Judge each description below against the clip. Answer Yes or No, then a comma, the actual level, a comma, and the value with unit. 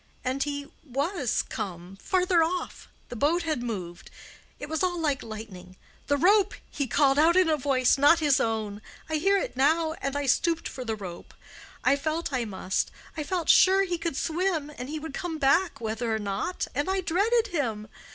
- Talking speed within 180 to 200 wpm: No, average, 170 wpm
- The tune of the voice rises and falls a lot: Yes, wide, 6.3 semitones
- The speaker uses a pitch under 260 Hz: No, very high, 290 Hz